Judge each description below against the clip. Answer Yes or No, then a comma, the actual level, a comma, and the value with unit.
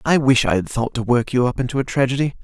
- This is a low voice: Yes, low, 125 Hz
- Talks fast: Yes, fast, 295 wpm